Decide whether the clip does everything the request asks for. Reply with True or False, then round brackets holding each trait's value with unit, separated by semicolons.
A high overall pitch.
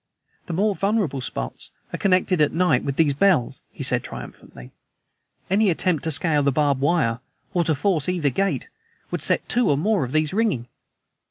False (160 Hz)